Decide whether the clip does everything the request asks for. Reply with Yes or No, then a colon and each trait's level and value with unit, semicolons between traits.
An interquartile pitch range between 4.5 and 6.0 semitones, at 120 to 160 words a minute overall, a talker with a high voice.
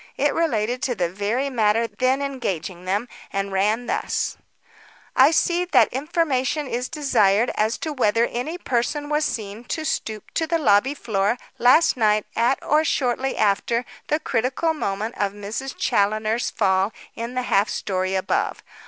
Yes: average, 4.8 semitones; average, 155 wpm; high, 235 Hz